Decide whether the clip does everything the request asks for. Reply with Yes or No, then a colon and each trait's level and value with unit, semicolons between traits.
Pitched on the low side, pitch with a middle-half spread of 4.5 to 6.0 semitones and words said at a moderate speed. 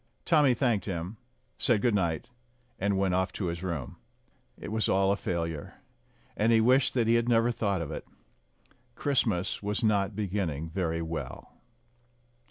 Yes: low, 100 Hz; average, 4.8 semitones; average, 160 wpm